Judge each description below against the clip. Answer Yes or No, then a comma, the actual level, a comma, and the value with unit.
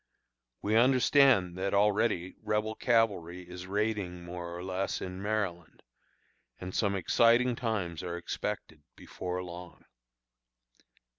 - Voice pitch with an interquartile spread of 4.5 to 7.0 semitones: No, average, 3.5 semitones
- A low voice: Yes, very low, 95 Hz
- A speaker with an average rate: No, slow, 115 wpm